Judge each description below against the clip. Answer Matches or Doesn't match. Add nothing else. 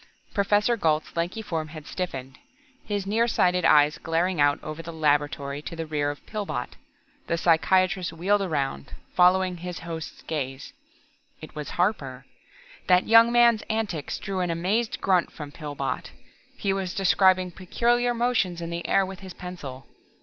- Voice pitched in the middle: Matches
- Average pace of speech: Matches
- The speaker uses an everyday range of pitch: Matches